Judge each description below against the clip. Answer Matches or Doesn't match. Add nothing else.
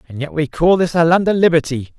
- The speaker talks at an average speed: Doesn't match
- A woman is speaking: Doesn't match